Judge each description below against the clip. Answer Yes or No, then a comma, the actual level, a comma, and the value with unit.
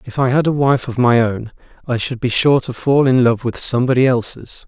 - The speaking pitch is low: Yes, low, 125 Hz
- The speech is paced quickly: Yes, fast, 245 wpm